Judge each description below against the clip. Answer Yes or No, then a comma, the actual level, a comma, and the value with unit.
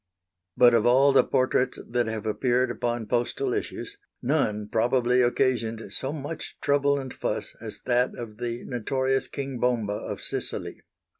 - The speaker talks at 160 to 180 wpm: No, average, 150 wpm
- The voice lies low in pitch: Yes, low, 125 Hz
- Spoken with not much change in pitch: Yes, narrow, 2.3 semitones